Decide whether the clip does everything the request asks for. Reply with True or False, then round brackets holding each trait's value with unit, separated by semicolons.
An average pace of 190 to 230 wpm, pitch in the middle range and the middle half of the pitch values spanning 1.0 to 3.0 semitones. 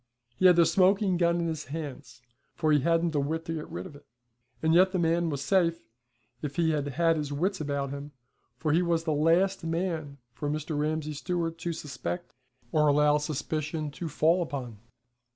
True (195 wpm; 160 Hz; 2.6 semitones)